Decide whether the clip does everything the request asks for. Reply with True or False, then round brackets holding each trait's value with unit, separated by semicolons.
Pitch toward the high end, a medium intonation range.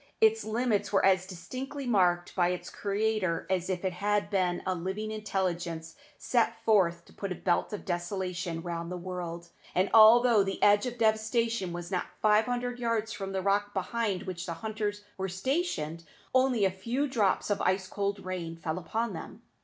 True (195 Hz; 3.5 semitones)